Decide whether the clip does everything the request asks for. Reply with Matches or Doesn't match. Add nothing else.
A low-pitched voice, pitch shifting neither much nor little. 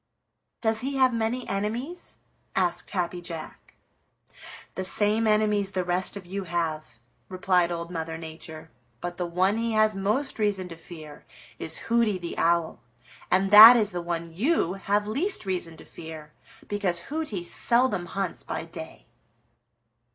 Doesn't match